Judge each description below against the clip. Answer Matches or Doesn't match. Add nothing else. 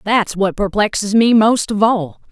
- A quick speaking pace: Doesn't match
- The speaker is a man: Doesn't match